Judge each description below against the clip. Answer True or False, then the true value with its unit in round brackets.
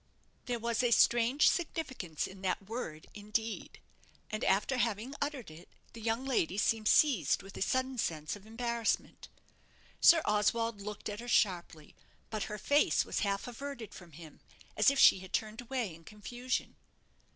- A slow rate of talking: False (165 wpm)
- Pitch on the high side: True (220 Hz)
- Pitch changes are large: False (4.0 semitones)